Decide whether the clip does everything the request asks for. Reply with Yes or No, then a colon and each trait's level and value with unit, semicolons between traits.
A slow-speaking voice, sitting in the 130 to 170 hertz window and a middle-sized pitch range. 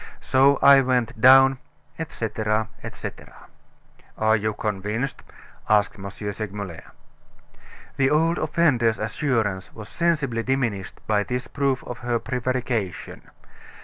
No: slow, 110 wpm; low, 120 Hz; average, 3.9 semitones